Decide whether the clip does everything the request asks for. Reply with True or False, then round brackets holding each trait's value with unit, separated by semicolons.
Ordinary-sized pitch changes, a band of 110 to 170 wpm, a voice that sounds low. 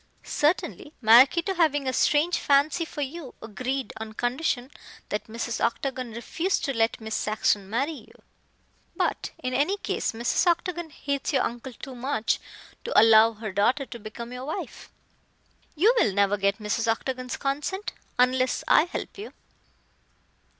False (4.7 semitones; 150 wpm; 255 Hz)